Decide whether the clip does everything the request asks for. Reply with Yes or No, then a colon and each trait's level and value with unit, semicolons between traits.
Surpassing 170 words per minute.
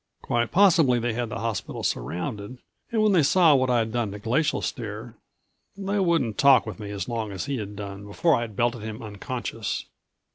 Yes: average, 190 wpm